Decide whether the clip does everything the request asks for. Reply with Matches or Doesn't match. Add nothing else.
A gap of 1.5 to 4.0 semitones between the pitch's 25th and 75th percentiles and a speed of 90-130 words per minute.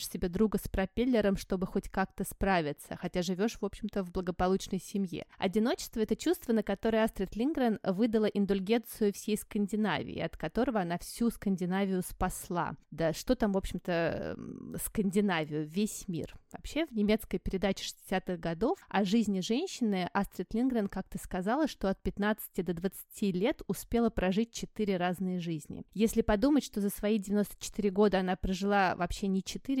Doesn't match